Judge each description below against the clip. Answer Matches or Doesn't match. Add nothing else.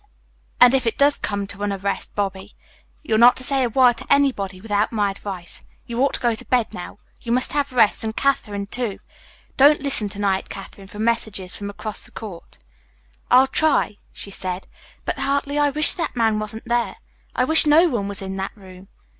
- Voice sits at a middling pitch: Doesn't match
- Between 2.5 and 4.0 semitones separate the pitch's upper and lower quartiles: Doesn't match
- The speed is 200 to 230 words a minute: Matches